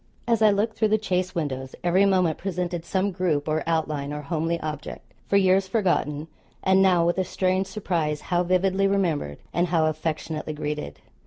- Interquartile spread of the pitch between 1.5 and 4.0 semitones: Yes, average, 3.6 semitones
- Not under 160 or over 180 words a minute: Yes, average, 175 wpm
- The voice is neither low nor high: Yes, medium, 175 Hz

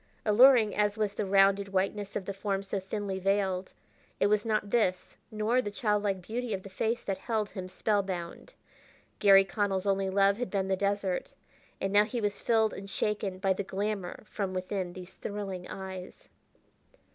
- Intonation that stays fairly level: Yes, narrow, 1.7 semitones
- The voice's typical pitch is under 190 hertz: No, high, 200 Hz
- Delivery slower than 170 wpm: No, average, 175 wpm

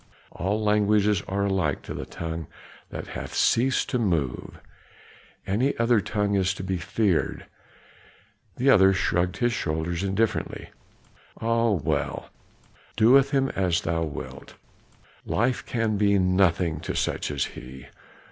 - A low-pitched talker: Yes, low, 100 Hz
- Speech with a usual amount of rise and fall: Yes, average, 4.5 semitones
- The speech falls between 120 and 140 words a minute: Yes, slow, 135 wpm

